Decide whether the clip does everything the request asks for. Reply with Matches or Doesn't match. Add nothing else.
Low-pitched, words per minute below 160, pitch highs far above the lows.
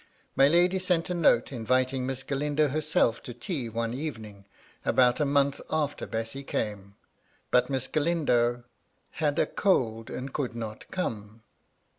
Doesn't match